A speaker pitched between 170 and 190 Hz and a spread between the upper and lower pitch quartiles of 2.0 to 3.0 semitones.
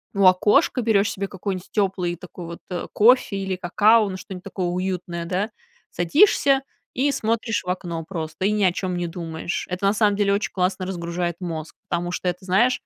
Yes: medium, 185 Hz; average, 2.7 semitones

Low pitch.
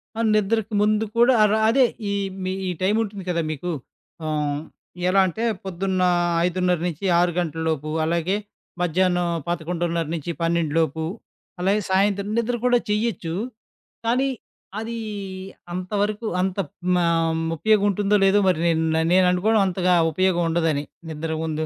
No: medium, 185 Hz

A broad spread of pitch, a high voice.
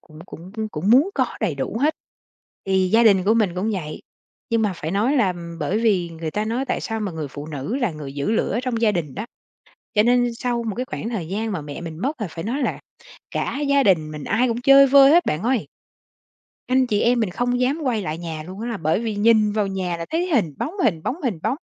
Yes: wide, 6.2 semitones; high, 215 Hz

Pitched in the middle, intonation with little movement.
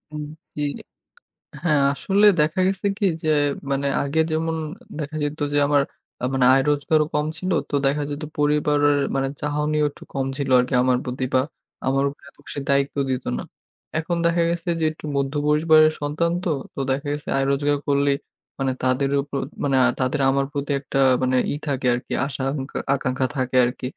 Yes: medium, 145 Hz; narrow, 2.0 semitones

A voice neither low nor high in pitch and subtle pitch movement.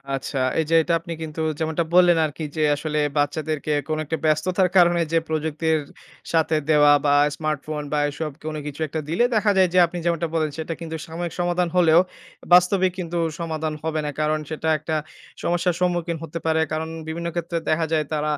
Yes: medium, 160 Hz; narrow, 1.9 semitones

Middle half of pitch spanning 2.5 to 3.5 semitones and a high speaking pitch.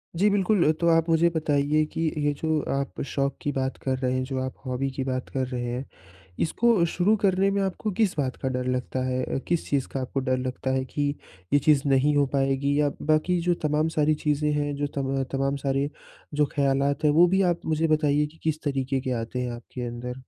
No: average, 3.0 semitones; medium, 145 Hz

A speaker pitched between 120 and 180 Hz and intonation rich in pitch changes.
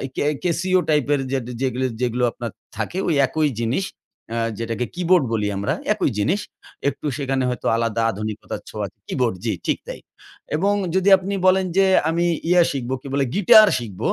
Yes: medium, 140 Hz; wide, 7.4 semitones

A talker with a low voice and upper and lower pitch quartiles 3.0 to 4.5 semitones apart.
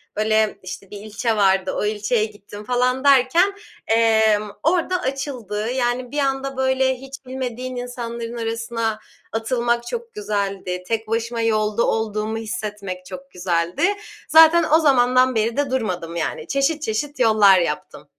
No: high, 230 Hz; average, 3.7 semitones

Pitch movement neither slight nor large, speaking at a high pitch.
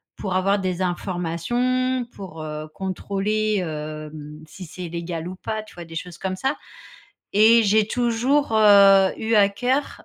Yes: average, 4.2 semitones; high, 195 Hz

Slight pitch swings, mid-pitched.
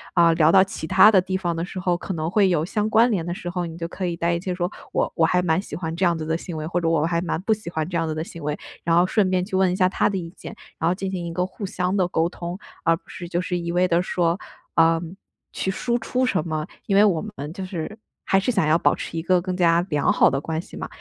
Yes: narrow, 2.2 semitones; medium, 175 Hz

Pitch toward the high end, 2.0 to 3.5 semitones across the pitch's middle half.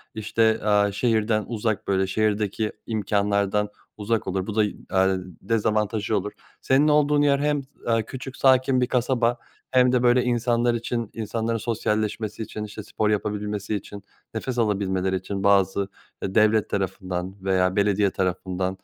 No: low, 105 Hz; average, 2.8 semitones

